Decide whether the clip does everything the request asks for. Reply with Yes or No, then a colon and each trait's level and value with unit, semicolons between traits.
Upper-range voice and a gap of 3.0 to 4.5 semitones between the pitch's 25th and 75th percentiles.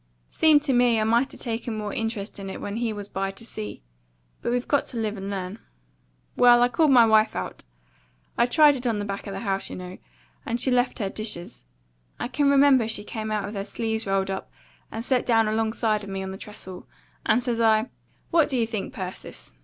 Yes: high, 220 Hz; average, 3.4 semitones